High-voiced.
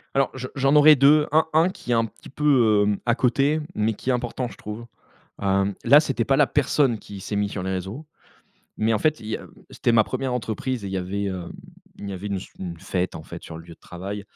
No: low, 115 Hz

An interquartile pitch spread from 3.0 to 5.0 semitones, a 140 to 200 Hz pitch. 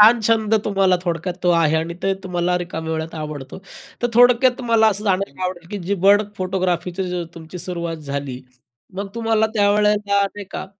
Yes: average, 3.5 semitones; medium, 185 Hz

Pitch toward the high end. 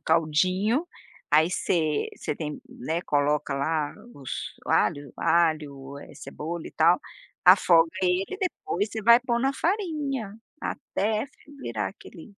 No: medium, 170 Hz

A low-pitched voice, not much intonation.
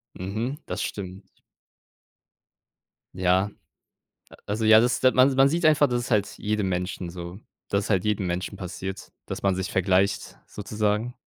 No: low, 100 Hz; average, 3.5 semitones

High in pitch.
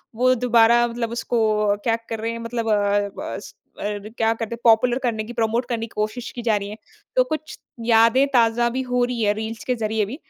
Yes: high, 230 Hz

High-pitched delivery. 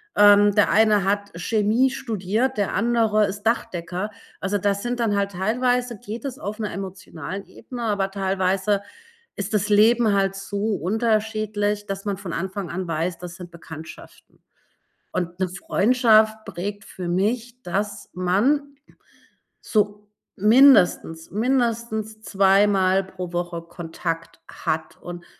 Yes: high, 205 Hz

